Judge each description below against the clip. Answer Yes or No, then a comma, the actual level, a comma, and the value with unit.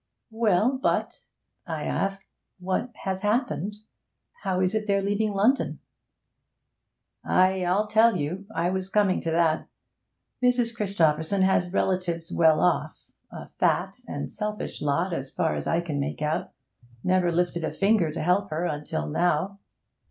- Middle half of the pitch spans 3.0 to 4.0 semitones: Yes, average, 3.5 semitones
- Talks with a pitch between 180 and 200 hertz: Yes, medium, 185 Hz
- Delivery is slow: No, average, 145 wpm